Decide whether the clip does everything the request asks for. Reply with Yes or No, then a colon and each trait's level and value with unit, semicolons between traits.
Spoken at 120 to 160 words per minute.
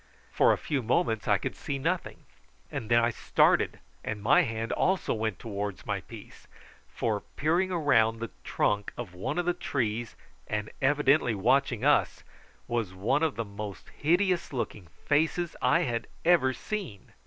Yes: average, 155 wpm